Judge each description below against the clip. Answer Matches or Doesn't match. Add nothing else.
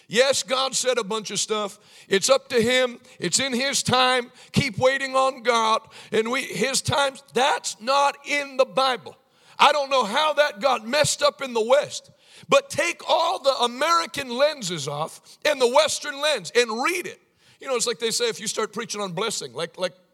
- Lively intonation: Doesn't match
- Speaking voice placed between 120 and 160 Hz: Doesn't match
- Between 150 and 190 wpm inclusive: Doesn't match